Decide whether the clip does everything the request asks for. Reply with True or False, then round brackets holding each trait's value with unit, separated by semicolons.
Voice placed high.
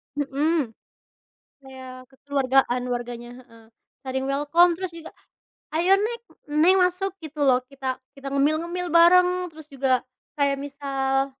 True (280 Hz)